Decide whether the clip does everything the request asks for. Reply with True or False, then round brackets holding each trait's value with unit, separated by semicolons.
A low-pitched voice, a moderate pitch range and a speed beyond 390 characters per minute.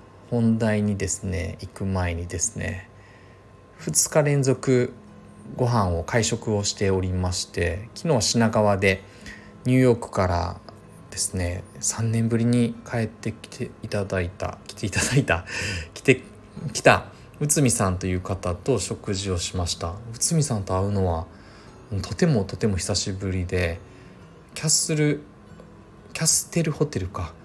False (105 Hz; 3.7 semitones; 275 characters per minute)